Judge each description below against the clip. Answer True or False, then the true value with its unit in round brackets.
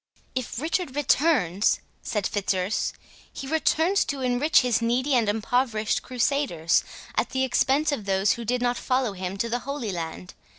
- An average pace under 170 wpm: True (160 wpm)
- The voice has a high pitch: True (245 Hz)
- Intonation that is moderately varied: True (5.0 semitones)